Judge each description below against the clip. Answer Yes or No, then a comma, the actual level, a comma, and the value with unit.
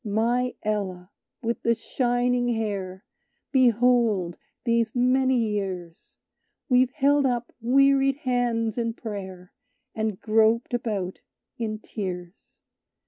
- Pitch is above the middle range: Yes, high, 230 Hz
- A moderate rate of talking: No, slow, 100 wpm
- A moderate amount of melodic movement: Yes, average, 3.2 semitones